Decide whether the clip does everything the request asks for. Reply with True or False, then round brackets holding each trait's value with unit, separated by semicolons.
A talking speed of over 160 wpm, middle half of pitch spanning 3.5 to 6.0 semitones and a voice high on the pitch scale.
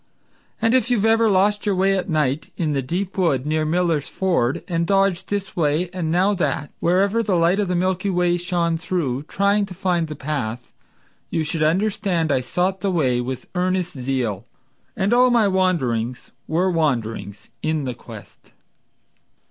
False (175 wpm; 4.6 semitones; 175 Hz)